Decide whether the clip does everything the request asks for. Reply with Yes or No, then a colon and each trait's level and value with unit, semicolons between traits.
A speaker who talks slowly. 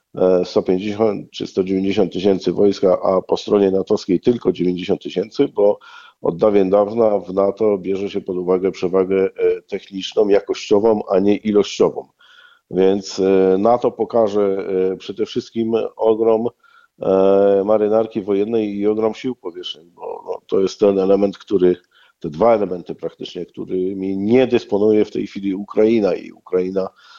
No: average, 130 wpm